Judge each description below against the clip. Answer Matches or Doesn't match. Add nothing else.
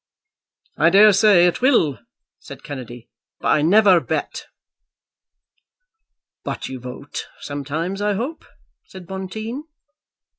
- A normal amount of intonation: Doesn't match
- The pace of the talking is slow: Matches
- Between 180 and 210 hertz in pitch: Matches